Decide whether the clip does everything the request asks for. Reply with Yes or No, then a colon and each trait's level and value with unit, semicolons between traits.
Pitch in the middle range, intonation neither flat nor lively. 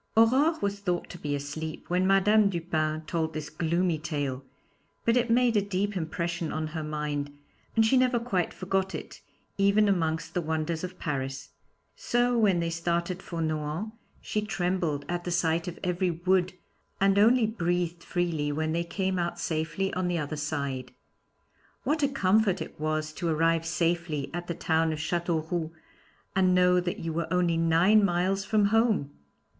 Yes: medium, 175 Hz; average, 3.6 semitones